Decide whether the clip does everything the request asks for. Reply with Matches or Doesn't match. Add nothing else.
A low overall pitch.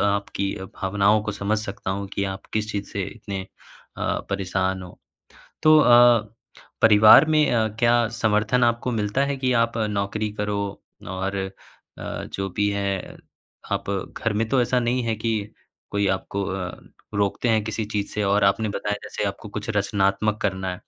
Matches